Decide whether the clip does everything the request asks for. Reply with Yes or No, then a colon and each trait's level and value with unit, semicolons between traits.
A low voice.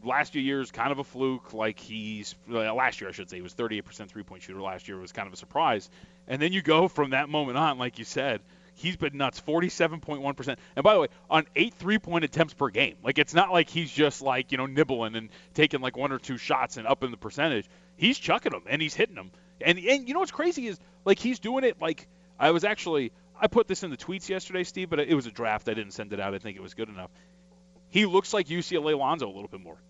No: medium, 150 Hz